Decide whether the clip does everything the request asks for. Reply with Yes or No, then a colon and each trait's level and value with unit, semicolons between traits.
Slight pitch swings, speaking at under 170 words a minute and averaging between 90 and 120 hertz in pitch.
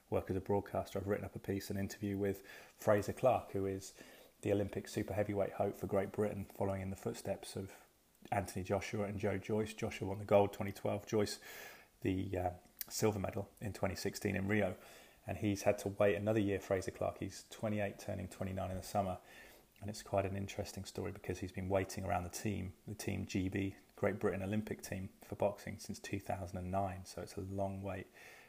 No: narrow, 1.1 semitones; average, 195 wpm; low, 100 Hz